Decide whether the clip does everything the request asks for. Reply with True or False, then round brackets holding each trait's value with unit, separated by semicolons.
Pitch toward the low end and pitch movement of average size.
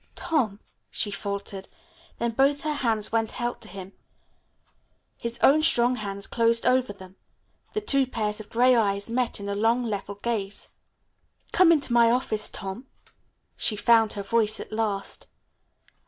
False (225 Hz; 3.4 semitones)